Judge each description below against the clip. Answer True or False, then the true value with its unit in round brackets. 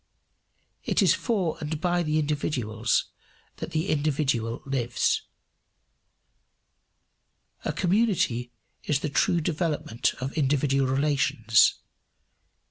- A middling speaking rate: False (95 wpm)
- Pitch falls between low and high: True (145 Hz)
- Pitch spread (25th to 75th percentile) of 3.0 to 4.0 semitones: True (3.5 semitones)